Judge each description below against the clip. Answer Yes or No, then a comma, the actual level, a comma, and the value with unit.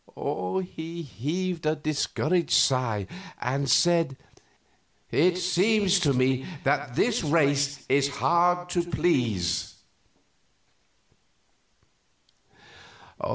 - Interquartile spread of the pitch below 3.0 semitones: No, average, 4.4 semitones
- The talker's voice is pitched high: No, medium, 155 Hz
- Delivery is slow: Yes, slow, 80 wpm